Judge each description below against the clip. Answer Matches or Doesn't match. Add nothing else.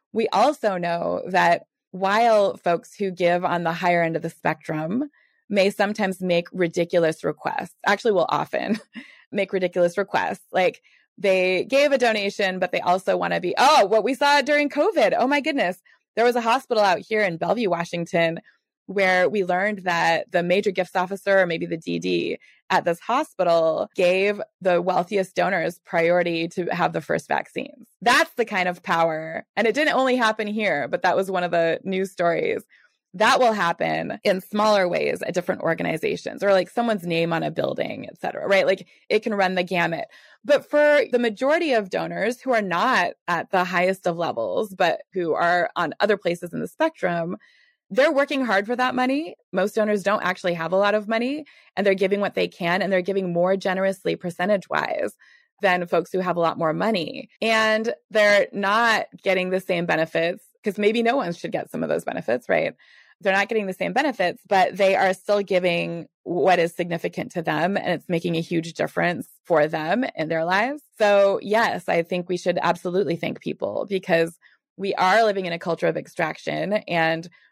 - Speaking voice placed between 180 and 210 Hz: Matches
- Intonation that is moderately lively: Matches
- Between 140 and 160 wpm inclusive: Doesn't match